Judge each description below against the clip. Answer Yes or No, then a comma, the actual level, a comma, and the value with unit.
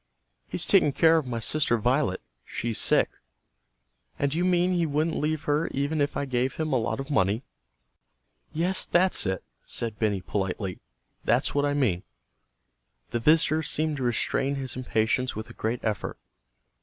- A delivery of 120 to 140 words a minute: No, average, 165 wpm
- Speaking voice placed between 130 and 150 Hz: Yes, low, 135 Hz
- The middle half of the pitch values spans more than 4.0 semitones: Yes, average, 5.3 semitones